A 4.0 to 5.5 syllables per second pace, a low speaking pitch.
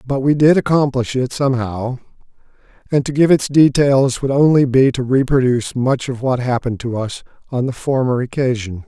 Yes: 5.3 syllables/s; low, 130 Hz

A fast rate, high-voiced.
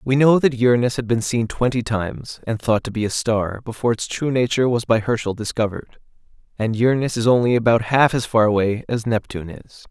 No: fast, 210 wpm; low, 115 Hz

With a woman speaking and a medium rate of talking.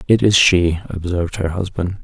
No: male; average, 175 wpm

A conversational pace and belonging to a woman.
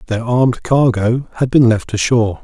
No: average, 175 wpm; male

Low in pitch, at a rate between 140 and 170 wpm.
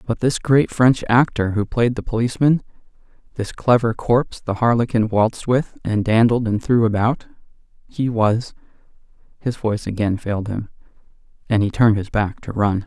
Yes: low, 115 Hz; average, 155 wpm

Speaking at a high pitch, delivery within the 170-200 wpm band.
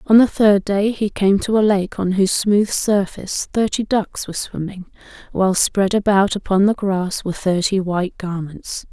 Yes: high, 195 Hz; average, 180 wpm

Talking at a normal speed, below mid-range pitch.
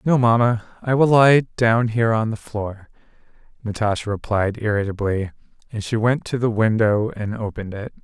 Yes: average, 165 wpm; low, 110 Hz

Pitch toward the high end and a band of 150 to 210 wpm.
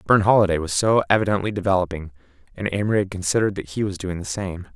No: very low, 95 Hz; average, 190 wpm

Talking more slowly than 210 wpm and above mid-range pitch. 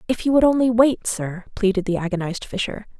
Yes: average, 200 wpm; high, 215 Hz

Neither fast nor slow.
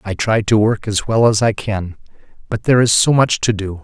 No: fast, 250 wpm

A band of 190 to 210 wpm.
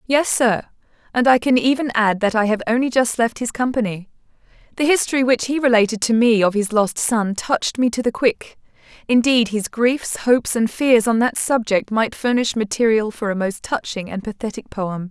Yes: average, 200 wpm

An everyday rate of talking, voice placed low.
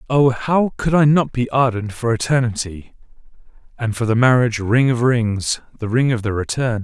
Yes: average, 175 wpm; low, 120 Hz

